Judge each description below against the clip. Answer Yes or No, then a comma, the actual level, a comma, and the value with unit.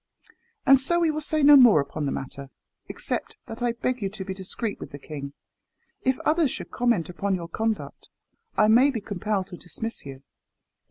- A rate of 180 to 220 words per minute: Yes, average, 195 wpm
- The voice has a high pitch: Yes, high, 215 Hz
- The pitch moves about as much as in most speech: No, wide, 6.7 semitones